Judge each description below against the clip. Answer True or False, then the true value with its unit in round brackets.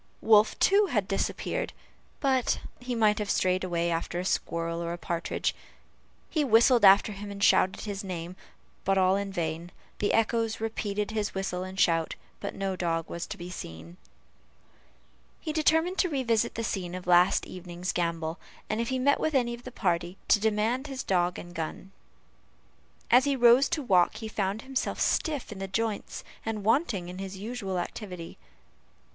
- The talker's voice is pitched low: False (200 Hz)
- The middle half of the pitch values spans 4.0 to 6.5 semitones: True (4.7 semitones)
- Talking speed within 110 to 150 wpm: False (175 wpm)